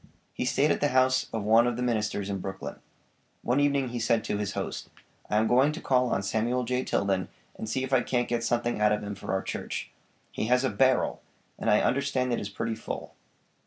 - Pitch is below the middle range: Yes, low, 120 Hz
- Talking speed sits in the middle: No, fast, 230 wpm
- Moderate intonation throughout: Yes, average, 3.2 semitones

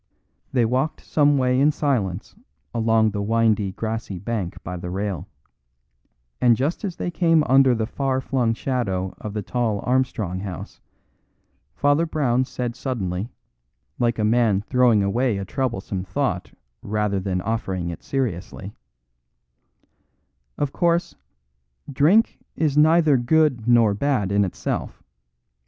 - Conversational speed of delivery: No, slow, 130 wpm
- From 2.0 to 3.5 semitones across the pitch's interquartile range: No, average, 4.9 semitones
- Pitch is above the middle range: No, low, 115 Hz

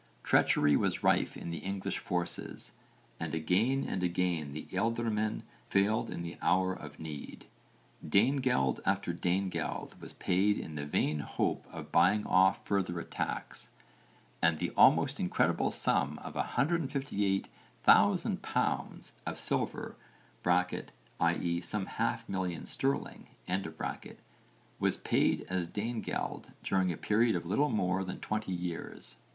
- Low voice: Yes, very low, 95 Hz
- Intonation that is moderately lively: Yes, average, 3.8 semitones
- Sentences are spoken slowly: Yes, slow, 125 wpm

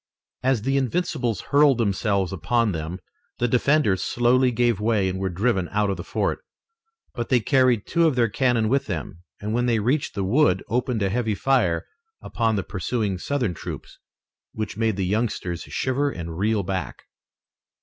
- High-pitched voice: No, low, 110 Hz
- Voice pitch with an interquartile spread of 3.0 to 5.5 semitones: Yes, average, 4.6 semitones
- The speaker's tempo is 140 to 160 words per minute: No, average, 170 wpm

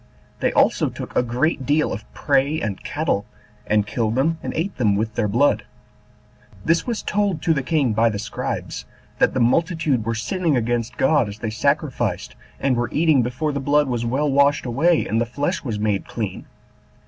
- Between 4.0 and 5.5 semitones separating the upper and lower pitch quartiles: Yes, average, 5.2 semitones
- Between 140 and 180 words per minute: No, average, 190 wpm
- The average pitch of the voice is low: Yes, low, 130 Hz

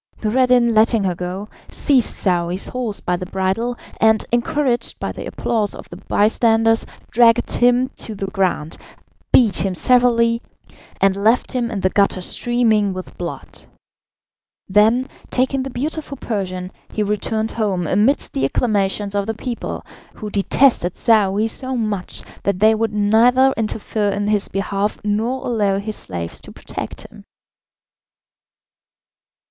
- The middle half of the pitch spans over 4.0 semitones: No, average, 3.5 semitones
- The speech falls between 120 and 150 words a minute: Yes, average, 140 wpm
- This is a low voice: No, high, 215 Hz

